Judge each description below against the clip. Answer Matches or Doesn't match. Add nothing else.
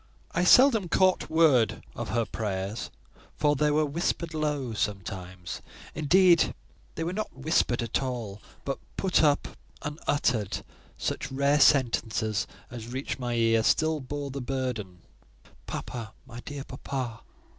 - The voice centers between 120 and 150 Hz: Matches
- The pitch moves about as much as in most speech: Matches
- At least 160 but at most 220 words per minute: Doesn't match